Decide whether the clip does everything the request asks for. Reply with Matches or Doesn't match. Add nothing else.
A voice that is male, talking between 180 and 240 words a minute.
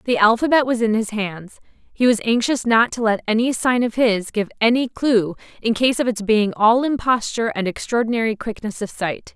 Doesn't match